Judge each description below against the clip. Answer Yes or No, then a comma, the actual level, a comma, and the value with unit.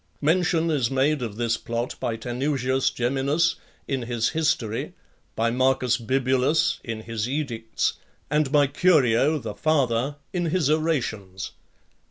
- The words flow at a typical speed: No, slow, 130 wpm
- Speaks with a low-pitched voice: Yes, low, 130 Hz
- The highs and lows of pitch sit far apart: No, average, 4.5 semitones